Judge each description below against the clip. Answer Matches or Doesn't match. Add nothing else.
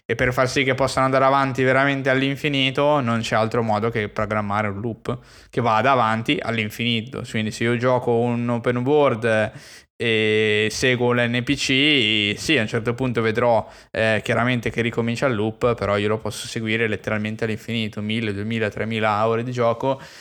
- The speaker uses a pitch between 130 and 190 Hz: Doesn't match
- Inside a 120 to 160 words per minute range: Doesn't match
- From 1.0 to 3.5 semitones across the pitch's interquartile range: Matches